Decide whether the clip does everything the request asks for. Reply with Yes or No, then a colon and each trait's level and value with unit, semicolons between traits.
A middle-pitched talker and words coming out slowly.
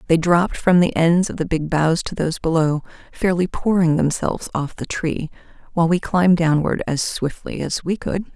No: medium, 170 Hz; average, 195 wpm